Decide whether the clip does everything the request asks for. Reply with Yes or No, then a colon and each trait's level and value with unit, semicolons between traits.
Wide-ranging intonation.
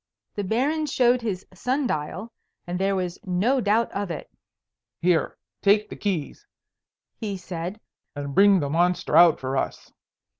No: average, 4.4 semitones